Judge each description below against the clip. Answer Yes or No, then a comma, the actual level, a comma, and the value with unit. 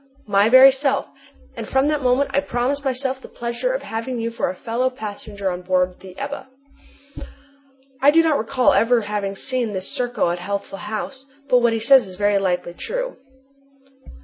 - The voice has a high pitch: Yes, high, 240 Hz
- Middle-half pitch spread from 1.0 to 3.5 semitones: No, average, 5.0 semitones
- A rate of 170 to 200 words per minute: Yes, average, 180 wpm